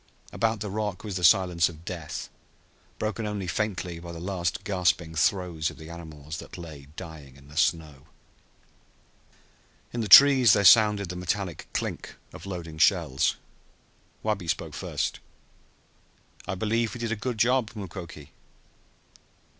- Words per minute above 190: No, average, 145 wpm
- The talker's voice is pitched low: Yes, very low, 90 Hz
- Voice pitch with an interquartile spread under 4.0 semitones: No, average, 4.5 semitones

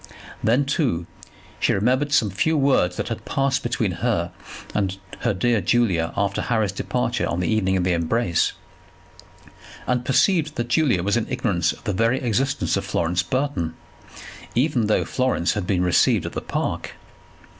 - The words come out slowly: No, average, 165 wpm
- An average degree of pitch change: No, wide, 6.2 semitones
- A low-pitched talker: Yes, low, 110 Hz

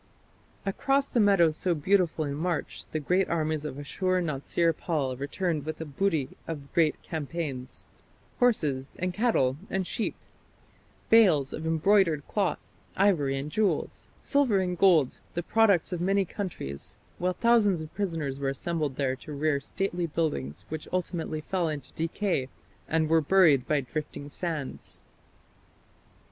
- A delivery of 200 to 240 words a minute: No, average, 145 wpm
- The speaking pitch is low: No, medium, 165 Hz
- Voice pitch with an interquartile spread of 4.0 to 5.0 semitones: Yes, average, 4.6 semitones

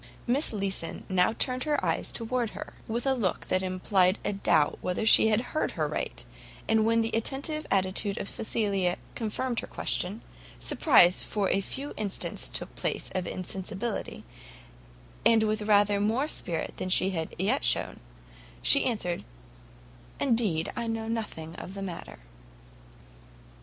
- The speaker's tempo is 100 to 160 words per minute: Yes, average, 145 wpm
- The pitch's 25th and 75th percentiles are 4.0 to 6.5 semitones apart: No, average, 3.6 semitones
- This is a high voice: Yes, high, 210 Hz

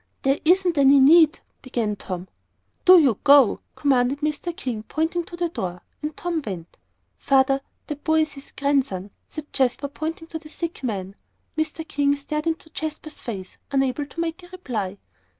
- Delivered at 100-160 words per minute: No, average, 170 wpm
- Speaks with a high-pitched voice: Yes, very high, 285 Hz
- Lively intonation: No, average, 4.0 semitones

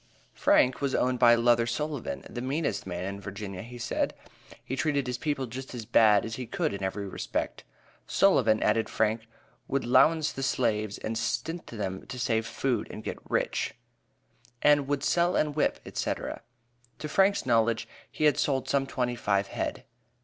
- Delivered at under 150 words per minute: No, average, 170 wpm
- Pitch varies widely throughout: No, average, 4.1 semitones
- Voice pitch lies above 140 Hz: No, low, 120 Hz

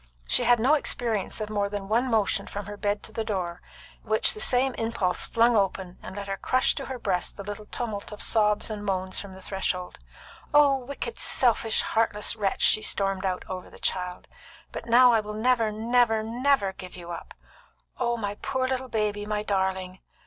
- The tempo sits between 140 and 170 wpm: No, average, 195 wpm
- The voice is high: Yes, high, 210 Hz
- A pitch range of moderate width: Yes, average, 3.2 semitones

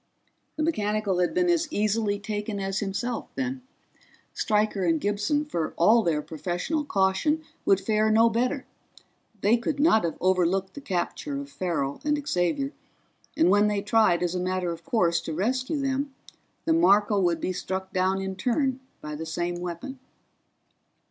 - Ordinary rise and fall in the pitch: No, wide, 6.4 semitones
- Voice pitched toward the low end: No, high, 205 Hz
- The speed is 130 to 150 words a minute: No, average, 160 wpm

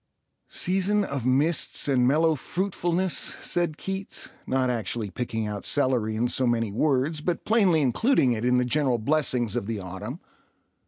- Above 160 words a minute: No, average, 155 wpm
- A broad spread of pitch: Yes, wide, 6.0 semitones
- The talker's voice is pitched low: Yes, low, 130 Hz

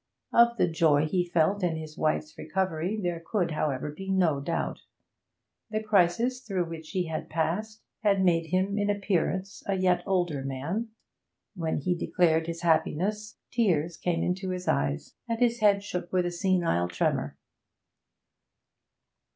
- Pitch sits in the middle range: Yes, medium, 180 Hz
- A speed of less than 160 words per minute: Yes, average, 150 wpm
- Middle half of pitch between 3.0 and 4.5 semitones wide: Yes, average, 3.6 semitones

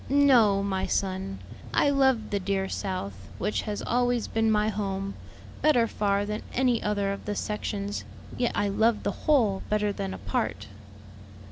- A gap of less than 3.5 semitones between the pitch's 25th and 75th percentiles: Yes, average, 2.7 semitones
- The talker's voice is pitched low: No, high, 210 Hz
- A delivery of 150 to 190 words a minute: Yes, average, 160 wpm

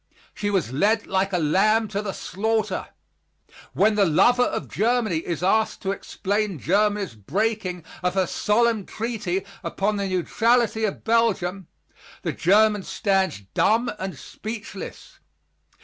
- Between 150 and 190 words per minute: No, slow, 135 wpm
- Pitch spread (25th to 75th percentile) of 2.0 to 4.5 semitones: Yes, average, 2.8 semitones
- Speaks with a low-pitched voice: No, high, 205 Hz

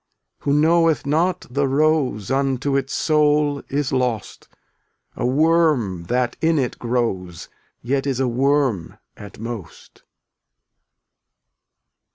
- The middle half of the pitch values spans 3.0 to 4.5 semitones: Yes, average, 3.7 semitones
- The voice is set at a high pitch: No, low, 135 Hz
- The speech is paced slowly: Yes, slow, 115 wpm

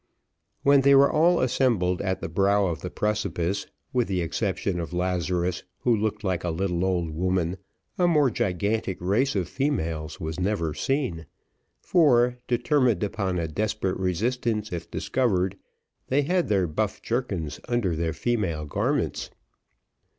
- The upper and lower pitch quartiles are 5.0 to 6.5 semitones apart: Yes, wide, 5.6 semitones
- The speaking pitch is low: Yes, low, 100 Hz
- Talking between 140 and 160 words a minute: Yes, average, 145 wpm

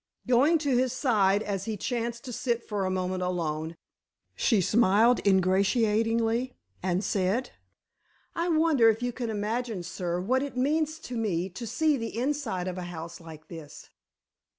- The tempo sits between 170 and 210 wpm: No, average, 160 wpm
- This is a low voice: No, high, 225 Hz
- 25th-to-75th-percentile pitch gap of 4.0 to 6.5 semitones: Yes, average, 5.1 semitones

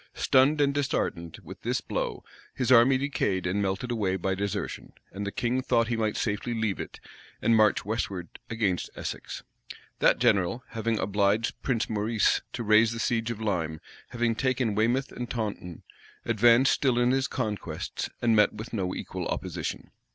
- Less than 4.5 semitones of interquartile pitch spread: Yes, average, 3.0 semitones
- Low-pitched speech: Yes, low, 110 Hz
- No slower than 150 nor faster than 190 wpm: Yes, average, 170 wpm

